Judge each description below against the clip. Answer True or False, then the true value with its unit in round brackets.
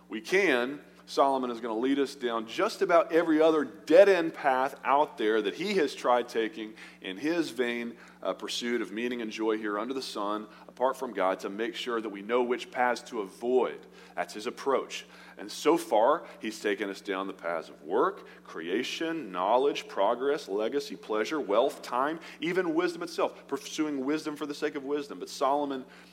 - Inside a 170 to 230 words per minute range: True (190 wpm)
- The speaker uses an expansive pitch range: True (6.4 semitones)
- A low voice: True (130 Hz)